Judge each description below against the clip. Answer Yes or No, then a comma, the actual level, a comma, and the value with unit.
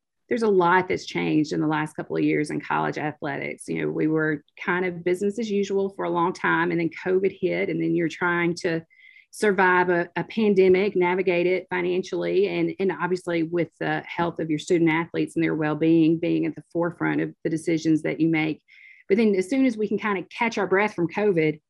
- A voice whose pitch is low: No, medium, 175 Hz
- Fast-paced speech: Yes, fast, 225 wpm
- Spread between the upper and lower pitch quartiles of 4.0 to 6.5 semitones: No, average, 2.8 semitones